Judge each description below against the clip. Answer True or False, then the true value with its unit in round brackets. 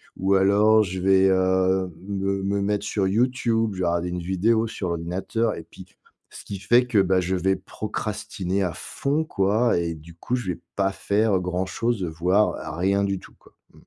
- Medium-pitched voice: False (95 Hz)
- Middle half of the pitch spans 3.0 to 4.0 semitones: False (2.5 semitones)